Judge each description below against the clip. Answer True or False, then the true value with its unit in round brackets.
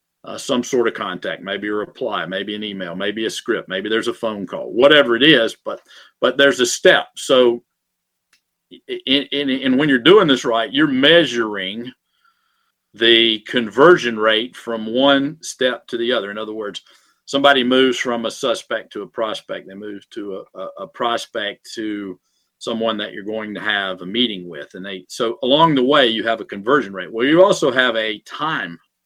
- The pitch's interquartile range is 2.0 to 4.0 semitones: False (4.8 semitones)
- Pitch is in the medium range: False (115 Hz)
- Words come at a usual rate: True (190 wpm)